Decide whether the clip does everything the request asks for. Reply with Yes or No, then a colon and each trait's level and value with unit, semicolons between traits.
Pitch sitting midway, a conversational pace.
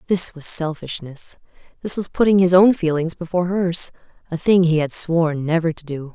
Yes: medium, 170 Hz; average, 175 wpm